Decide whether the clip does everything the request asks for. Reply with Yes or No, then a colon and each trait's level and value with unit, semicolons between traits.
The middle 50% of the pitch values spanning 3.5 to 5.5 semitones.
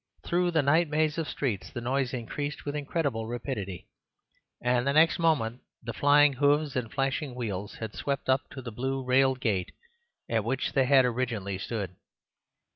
Yes: average, 3.8 semitones